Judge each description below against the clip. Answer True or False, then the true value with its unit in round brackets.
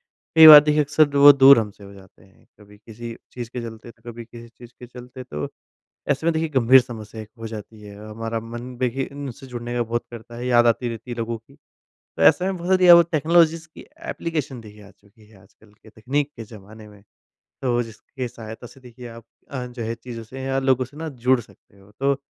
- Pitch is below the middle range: True (120 Hz)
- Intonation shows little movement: False (3.3 semitones)